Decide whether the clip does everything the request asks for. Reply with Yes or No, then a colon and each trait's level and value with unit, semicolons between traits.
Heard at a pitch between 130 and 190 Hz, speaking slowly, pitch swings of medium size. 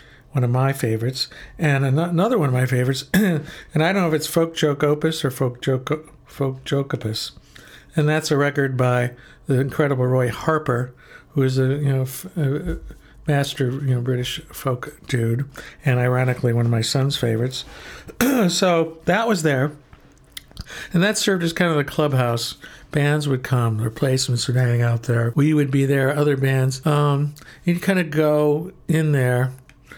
No: medium, 140 Hz; average, 175 wpm; average, 3.2 semitones